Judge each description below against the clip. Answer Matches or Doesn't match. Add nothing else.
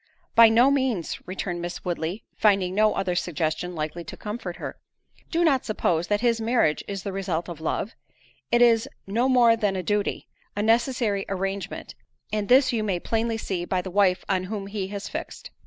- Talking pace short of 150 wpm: Doesn't match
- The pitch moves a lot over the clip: Doesn't match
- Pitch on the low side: Doesn't match